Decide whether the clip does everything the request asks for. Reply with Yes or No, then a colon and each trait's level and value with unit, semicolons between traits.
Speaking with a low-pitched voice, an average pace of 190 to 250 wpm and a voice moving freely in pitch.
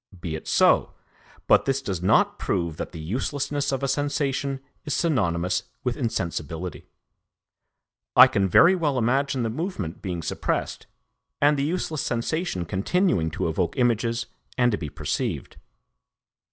No: low, 120 Hz; average, 140 wpm; wide, 8.0 semitones